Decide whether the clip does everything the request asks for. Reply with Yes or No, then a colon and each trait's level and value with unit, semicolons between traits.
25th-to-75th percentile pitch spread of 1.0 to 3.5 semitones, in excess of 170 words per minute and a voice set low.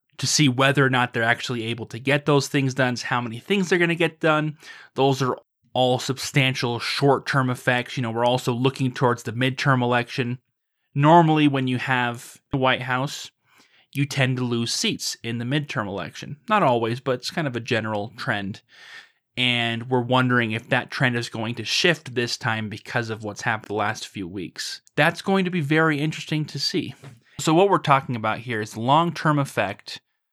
Yes: average, 3.1 semitones; average, 195 wpm; low, 130 Hz